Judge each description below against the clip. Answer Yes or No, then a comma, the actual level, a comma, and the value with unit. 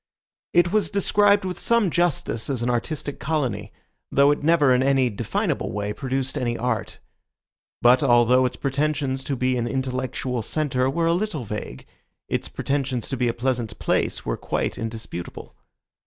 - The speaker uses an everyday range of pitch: Yes, average, 4.0 semitones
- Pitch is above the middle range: No, low, 130 Hz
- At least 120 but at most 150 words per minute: No, average, 160 wpm